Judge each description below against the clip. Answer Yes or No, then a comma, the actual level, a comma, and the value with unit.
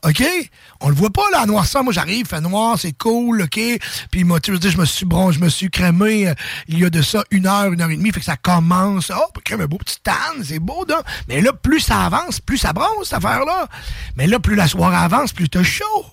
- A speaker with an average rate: No, fast, 270 wpm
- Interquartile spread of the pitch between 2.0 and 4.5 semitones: No, average, 5.0 semitones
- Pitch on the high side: Yes, high, 195 Hz